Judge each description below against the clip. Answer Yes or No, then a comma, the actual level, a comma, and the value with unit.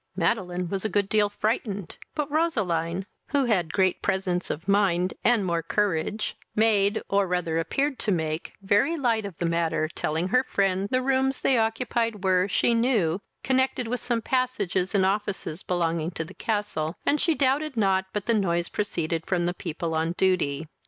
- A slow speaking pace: No, average, 175 wpm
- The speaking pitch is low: No, high, 195 Hz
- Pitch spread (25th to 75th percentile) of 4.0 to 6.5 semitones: Yes, average, 4.9 semitones